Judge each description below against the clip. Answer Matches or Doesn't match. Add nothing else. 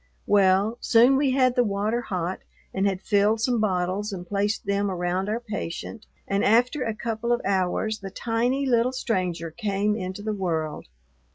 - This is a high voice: Matches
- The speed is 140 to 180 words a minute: Matches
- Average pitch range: Matches